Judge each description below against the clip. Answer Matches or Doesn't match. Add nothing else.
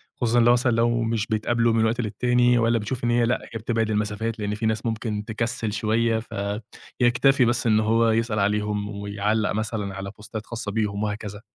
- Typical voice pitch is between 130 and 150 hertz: Doesn't match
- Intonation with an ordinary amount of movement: Doesn't match